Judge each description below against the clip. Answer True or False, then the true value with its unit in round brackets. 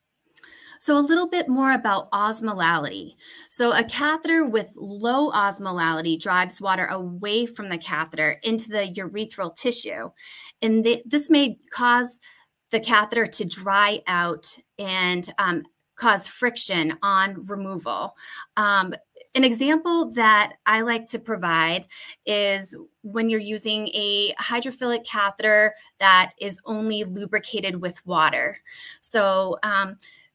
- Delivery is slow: True (125 wpm)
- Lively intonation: False (4.1 semitones)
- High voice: True (215 Hz)